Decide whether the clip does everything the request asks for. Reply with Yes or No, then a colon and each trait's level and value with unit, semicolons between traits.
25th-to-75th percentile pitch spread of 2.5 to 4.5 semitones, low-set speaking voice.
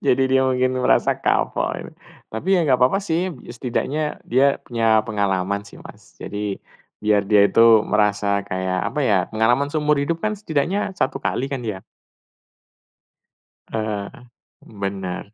No: wide, 5.5 semitones; low, 115 Hz